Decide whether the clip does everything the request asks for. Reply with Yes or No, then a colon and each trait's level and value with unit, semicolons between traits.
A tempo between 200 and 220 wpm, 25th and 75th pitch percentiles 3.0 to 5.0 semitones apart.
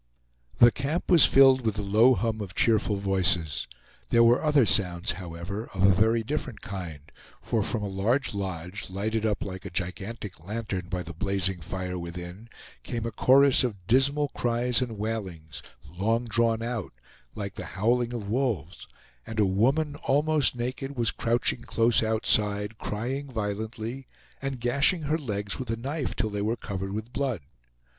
No: average, 165 wpm; average, 4.1 semitones